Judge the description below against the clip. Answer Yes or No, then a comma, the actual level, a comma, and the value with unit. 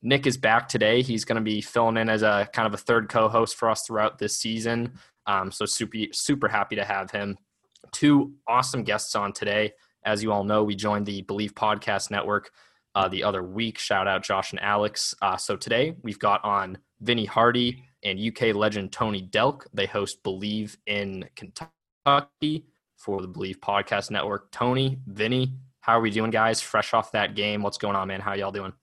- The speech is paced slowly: No, average, 200 wpm